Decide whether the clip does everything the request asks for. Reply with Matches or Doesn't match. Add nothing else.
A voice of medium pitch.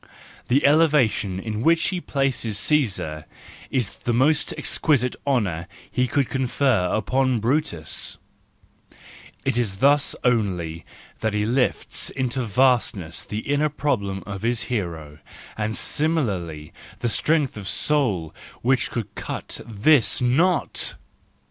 Doesn't match